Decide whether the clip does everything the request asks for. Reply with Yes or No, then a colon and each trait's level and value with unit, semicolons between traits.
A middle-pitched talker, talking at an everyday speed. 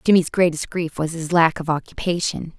Yes: medium, 165 Hz; average, 185 wpm